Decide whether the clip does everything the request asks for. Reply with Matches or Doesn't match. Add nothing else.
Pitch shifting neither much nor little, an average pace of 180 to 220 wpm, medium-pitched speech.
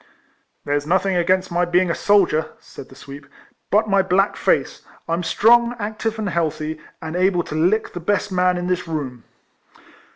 Matches